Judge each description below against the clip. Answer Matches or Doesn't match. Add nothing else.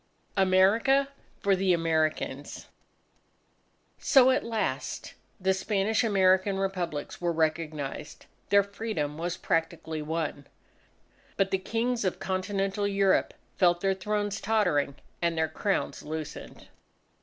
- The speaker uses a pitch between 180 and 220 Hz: Matches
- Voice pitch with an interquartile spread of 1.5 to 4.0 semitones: Matches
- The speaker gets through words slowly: Matches